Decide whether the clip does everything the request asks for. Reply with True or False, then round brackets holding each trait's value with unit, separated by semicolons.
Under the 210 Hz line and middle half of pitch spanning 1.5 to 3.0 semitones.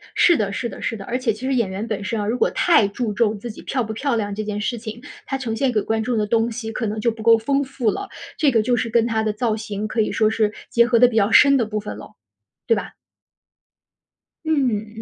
False (225 Hz; 2.5 semitones)